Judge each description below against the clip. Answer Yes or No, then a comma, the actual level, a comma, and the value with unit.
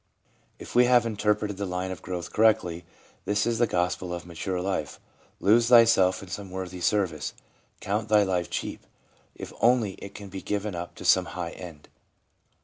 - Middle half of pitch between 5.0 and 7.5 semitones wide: No, average, 2.9 semitones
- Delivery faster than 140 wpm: Yes, average, 175 wpm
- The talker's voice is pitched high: No, very low, 95 Hz